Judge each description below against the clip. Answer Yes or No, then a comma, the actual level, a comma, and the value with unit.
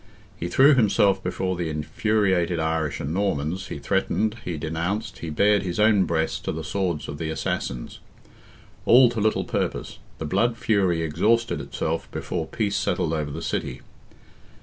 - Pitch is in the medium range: No, very low, 90 Hz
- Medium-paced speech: Yes, average, 160 wpm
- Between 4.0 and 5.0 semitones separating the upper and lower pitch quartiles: Yes, average, 4.6 semitones